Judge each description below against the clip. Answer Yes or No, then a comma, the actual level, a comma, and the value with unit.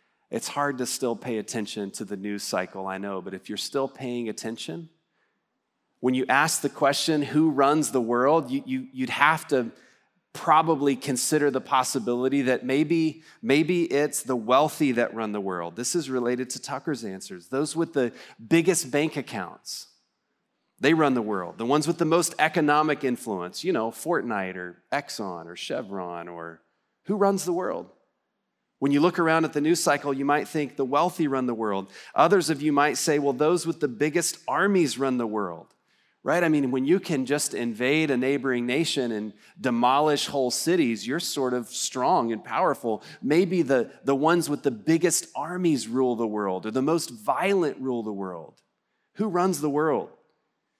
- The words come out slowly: No, average, 180 wpm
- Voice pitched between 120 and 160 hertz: Yes, medium, 140 Hz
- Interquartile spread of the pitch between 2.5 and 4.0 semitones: No, average, 4.9 semitones